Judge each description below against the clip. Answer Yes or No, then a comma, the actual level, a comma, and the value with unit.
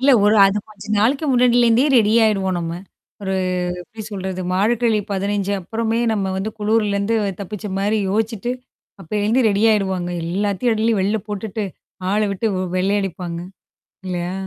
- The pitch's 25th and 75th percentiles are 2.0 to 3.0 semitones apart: Yes, narrow, 2.6 semitones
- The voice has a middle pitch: No, high, 205 Hz